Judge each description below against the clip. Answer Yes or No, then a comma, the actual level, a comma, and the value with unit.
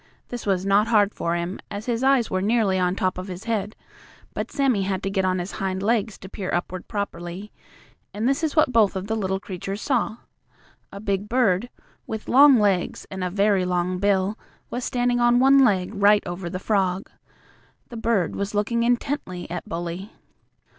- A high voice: Yes, high, 200 Hz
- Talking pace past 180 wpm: Yes, average, 190 wpm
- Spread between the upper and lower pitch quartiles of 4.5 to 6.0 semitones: No, average, 3.7 semitones